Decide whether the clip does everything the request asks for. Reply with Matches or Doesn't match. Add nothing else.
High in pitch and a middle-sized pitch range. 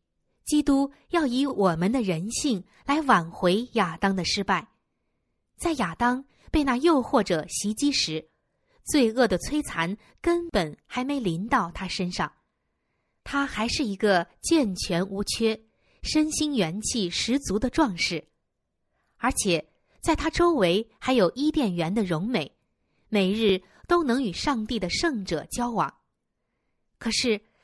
Doesn't match